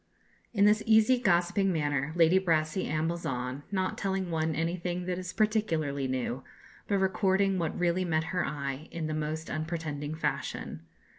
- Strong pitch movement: No, average, 3.5 semitones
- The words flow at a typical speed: Yes, average, 155 wpm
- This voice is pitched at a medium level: Yes, medium, 170 Hz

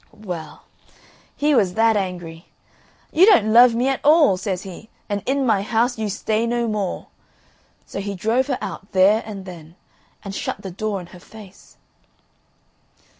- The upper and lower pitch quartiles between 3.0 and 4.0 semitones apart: Yes, average, 3.7 semitones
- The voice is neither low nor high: No, high, 210 Hz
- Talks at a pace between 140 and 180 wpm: Yes, average, 165 wpm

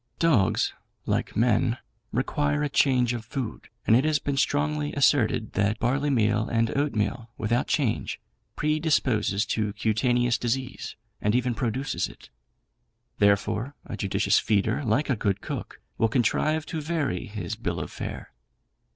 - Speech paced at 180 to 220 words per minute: No, average, 140 wpm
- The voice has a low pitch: Yes, low, 120 Hz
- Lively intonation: No, average, 4.9 semitones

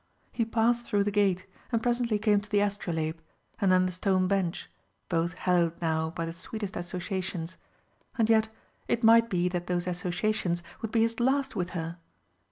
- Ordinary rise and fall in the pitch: Yes, average, 4.1 semitones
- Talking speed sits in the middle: Yes, average, 175 wpm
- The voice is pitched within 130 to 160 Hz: No, high, 190 Hz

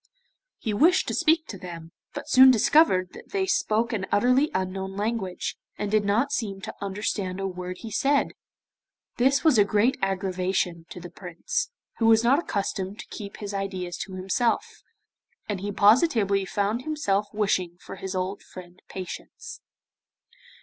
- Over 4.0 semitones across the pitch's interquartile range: Yes, average, 4.6 semitones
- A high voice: Yes, high, 205 Hz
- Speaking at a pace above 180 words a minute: No, average, 160 wpm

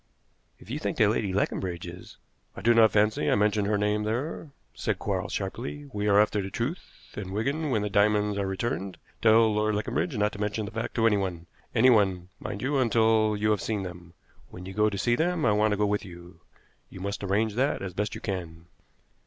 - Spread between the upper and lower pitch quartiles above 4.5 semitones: No, narrow, 2.4 semitones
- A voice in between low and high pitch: No, low, 105 Hz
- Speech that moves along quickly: Yes, fast, 215 wpm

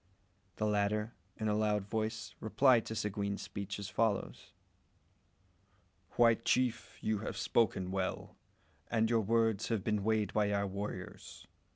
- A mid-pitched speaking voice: No, low, 105 Hz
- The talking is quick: No, average, 140 wpm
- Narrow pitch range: Yes, narrow, 1.8 semitones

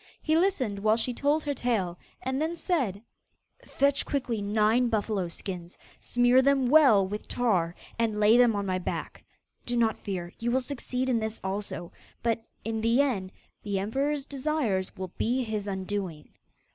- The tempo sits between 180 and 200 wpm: No, average, 165 wpm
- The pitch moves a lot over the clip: No, average, 4.7 semitones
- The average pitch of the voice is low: No, high, 225 Hz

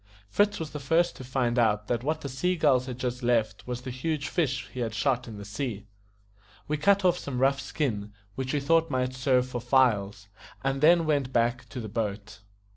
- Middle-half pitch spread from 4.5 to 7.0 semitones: No, average, 3.7 semitones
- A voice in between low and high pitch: No, low, 130 Hz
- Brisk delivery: Yes, fast, 210 wpm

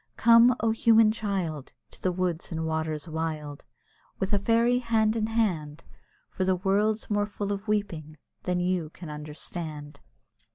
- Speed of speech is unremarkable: Yes, average, 155 wpm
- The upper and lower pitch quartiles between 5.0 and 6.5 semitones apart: Yes, wide, 5.4 semitones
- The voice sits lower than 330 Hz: Yes, medium, 185 Hz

